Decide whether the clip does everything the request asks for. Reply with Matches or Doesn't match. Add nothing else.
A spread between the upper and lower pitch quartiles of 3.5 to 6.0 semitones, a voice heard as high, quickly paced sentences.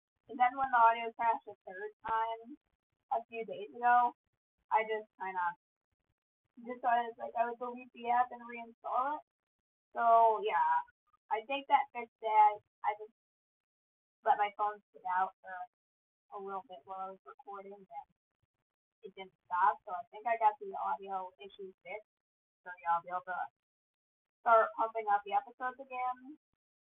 Doesn't match